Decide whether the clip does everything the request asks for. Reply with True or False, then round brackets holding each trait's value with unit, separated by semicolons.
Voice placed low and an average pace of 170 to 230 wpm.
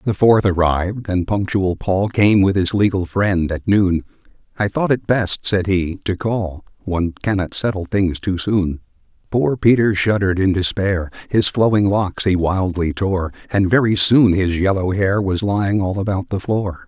True (95 Hz; 180 wpm)